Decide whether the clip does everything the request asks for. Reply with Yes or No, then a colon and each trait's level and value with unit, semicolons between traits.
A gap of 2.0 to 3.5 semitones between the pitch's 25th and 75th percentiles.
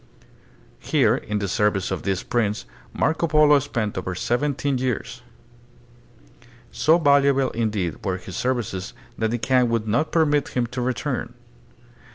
No: average, 5.2 semitones